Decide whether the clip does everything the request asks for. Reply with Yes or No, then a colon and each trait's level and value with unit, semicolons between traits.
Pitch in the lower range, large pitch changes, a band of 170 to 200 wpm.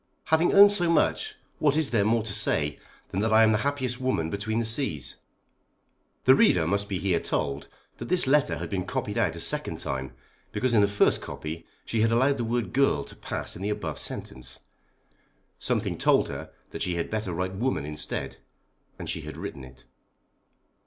Yes: low, 110 Hz; wide, 7.1 semitones; average, 195 wpm